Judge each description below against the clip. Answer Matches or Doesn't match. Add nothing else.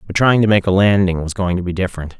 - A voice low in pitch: Matches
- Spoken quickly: Matches